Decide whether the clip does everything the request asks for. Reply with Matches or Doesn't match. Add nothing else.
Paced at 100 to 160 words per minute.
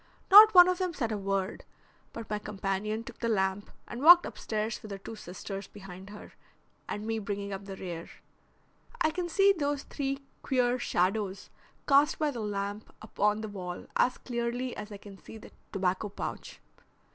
Doesn't match